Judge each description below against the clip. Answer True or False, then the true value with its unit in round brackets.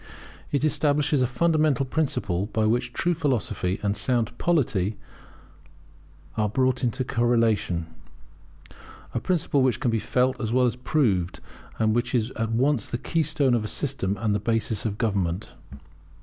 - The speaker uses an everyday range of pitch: True (4.2 semitones)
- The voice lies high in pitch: False (120 Hz)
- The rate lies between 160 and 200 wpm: False (150 wpm)